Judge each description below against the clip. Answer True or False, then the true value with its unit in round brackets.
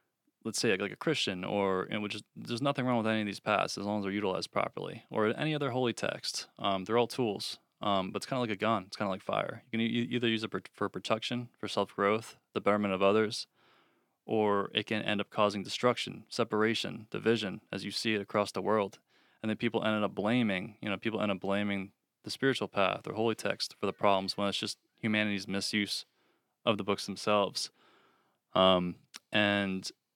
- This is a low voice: True (105 Hz)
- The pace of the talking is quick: True (215 wpm)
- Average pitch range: False (2.2 semitones)